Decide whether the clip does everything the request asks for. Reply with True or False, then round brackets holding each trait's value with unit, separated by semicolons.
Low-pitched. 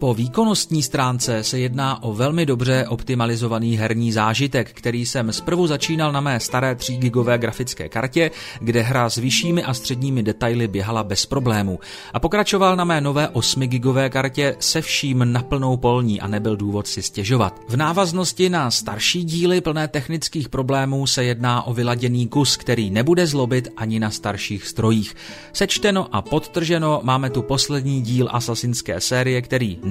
True (125 Hz)